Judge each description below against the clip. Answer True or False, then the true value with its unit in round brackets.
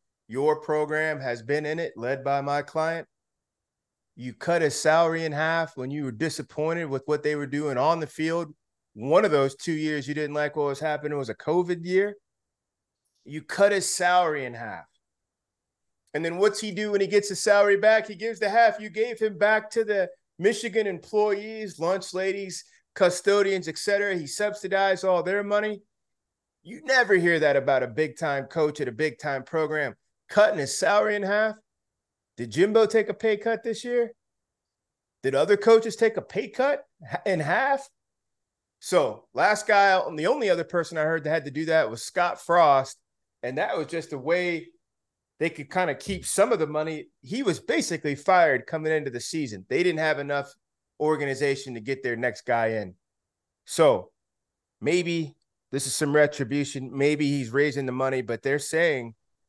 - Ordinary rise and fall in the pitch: False (6.0 semitones)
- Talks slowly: False (185 wpm)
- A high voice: False (160 Hz)